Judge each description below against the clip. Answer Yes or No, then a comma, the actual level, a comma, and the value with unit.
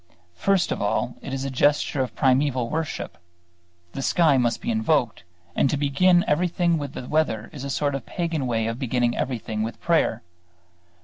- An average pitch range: Yes, average, 4.5 semitones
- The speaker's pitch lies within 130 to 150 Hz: Yes, low, 135 Hz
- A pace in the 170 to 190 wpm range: Yes, average, 180 wpm